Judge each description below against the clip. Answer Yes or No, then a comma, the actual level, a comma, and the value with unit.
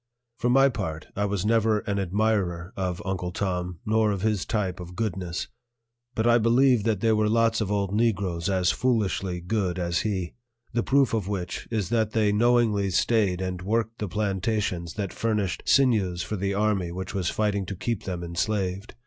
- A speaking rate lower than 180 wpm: No, average, 185 wpm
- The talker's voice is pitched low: Yes, low, 100 Hz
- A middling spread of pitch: Yes, average, 3.3 semitones